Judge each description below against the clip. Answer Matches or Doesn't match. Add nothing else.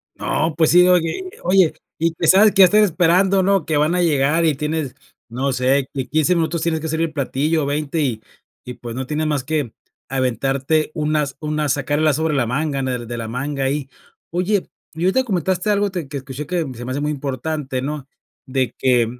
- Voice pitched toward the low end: Doesn't match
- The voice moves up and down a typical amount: Matches